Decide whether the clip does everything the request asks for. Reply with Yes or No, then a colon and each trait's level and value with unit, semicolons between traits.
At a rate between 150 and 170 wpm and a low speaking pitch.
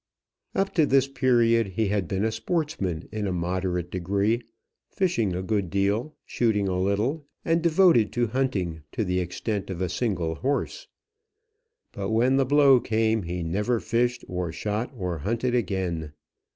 Yes: average, 160 wpm; low, 105 Hz